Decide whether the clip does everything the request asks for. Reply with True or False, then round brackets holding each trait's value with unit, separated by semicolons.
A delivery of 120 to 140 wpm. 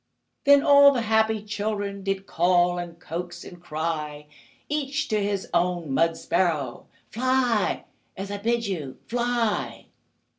True (135 wpm)